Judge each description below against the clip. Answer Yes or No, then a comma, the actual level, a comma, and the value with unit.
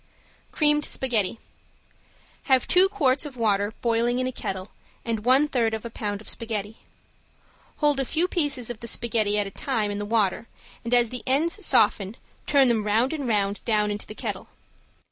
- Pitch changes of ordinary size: Yes, average, 4.1 semitones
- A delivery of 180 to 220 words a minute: Yes, average, 185 wpm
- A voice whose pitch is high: Yes, high, 235 Hz